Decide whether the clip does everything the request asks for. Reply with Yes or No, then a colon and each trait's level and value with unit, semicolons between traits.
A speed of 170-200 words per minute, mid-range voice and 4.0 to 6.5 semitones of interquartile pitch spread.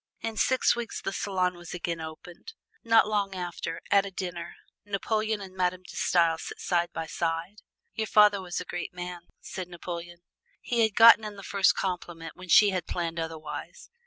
No: average, 185 wpm; medium, 180 Hz; average, 3.0 semitones